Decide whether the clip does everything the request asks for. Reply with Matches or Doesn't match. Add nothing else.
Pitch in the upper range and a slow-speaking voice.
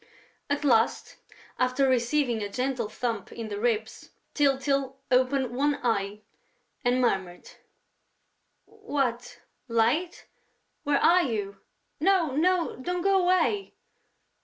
Matches